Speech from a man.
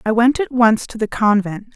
No: female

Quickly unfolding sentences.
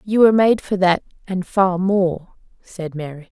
No: average, 175 wpm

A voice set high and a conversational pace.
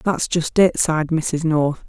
No: medium, 160 Hz; average, 190 wpm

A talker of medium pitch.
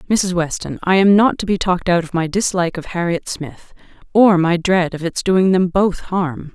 Yes: medium, 180 Hz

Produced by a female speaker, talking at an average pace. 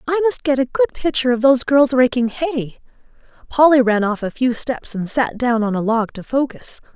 No: female; fast, 215 wpm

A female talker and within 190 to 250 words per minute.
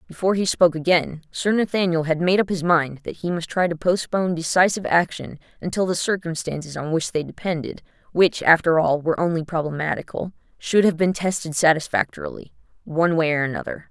No: female; average, 170 wpm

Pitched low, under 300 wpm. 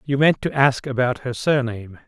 Yes: low, 130 Hz; average, 200 wpm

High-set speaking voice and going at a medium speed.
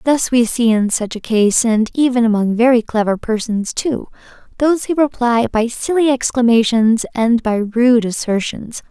Yes: high, 235 Hz; average, 160 wpm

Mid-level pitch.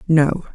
Yes: medium, 160 Hz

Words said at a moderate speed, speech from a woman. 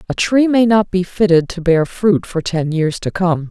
No: fast, 240 wpm; female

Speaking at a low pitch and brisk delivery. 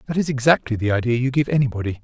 Yes: low, 125 Hz; fast, 235 wpm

